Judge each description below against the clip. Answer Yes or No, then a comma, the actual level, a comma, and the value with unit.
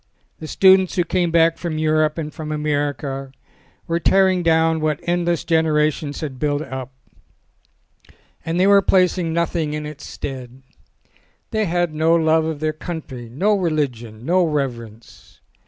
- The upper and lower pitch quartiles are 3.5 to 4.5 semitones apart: No, average, 2.8 semitones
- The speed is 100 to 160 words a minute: Yes, average, 150 wpm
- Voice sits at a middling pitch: Yes, medium, 155 Hz